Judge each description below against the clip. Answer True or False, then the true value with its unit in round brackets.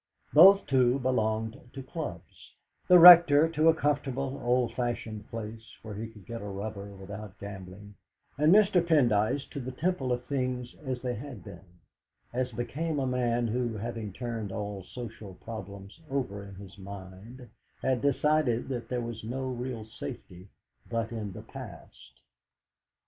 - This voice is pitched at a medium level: False (120 Hz)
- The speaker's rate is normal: True (155 wpm)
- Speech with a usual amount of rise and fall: True (4.2 semitones)